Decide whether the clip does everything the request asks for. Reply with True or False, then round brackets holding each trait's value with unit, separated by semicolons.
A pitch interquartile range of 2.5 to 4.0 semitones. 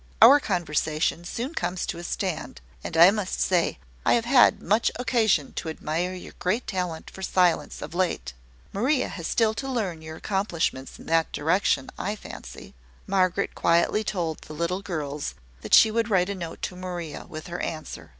False (4.4 semitones)